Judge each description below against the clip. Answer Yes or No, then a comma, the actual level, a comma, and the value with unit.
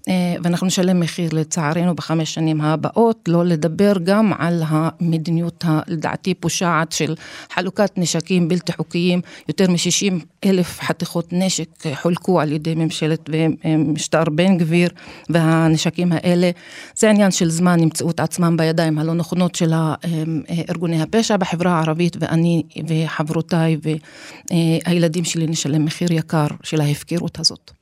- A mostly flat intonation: Yes, narrow, 1.8 semitones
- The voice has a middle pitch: Yes, medium, 170 Hz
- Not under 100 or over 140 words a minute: Yes, average, 125 wpm